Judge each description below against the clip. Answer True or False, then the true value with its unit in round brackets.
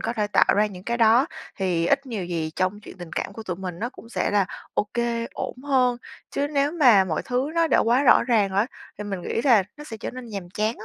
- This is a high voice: True (220 Hz)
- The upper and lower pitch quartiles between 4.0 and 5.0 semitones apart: True (4.7 semitones)